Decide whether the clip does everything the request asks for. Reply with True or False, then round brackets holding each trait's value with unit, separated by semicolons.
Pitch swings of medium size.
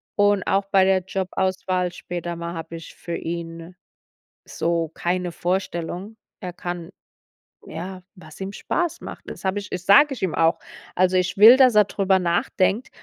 False (2.2 semitones)